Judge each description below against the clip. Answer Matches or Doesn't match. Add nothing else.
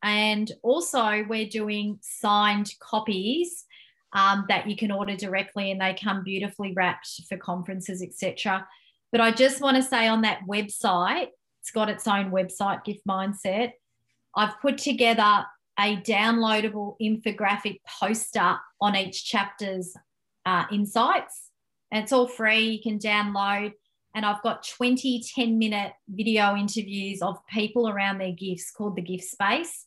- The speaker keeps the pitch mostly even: Matches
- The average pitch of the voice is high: Matches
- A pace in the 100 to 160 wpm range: Matches